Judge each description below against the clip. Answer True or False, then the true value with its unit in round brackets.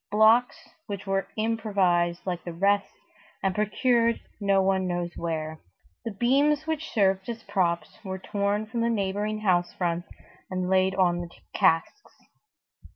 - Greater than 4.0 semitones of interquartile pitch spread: False (3.4 semitones)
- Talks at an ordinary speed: True (145 wpm)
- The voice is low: False (195 Hz)